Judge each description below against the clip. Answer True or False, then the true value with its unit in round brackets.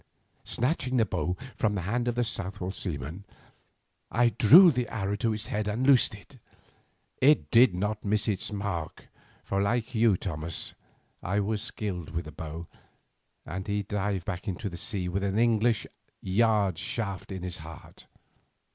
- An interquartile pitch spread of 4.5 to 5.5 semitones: False (3.8 semitones)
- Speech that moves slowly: False (160 wpm)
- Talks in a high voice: False (100 Hz)